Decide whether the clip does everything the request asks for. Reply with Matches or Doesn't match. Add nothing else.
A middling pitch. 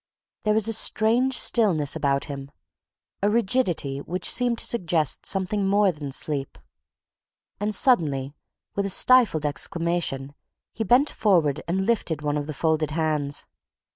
Matches